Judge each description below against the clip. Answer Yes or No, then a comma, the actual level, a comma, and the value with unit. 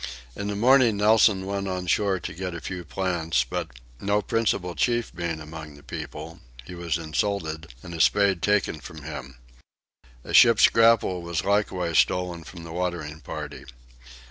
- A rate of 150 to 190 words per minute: Yes, average, 165 wpm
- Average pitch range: Yes, average, 3.9 semitones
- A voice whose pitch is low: Yes, very low, 90 Hz